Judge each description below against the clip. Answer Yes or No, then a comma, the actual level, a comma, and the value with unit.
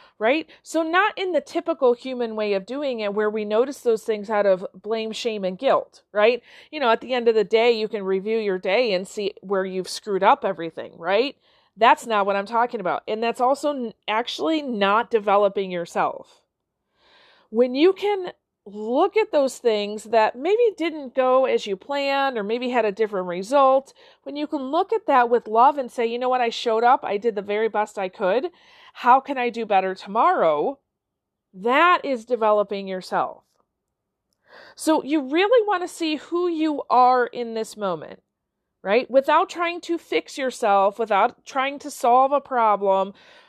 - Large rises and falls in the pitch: Yes, wide, 5.7 semitones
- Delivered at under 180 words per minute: No, average, 185 wpm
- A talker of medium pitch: No, high, 240 Hz